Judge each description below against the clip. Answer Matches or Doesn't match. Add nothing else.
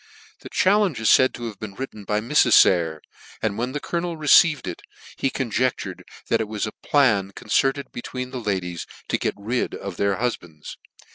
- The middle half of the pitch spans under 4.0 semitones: Doesn't match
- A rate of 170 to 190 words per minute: Matches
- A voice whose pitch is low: Matches